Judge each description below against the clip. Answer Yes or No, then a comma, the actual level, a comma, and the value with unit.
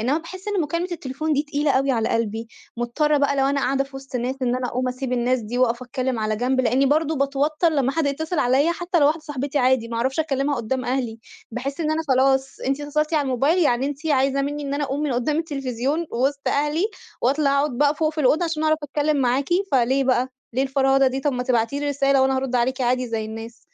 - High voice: Yes, very high, 270 Hz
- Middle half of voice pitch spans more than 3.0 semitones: No, narrow, 2.6 semitones